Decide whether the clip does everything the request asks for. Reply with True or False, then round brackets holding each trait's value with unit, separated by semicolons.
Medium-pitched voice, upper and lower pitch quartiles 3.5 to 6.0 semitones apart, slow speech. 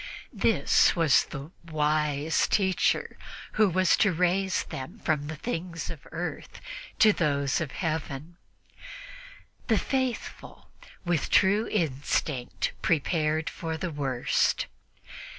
True (160 Hz; 3.9 semitones; 110 wpm)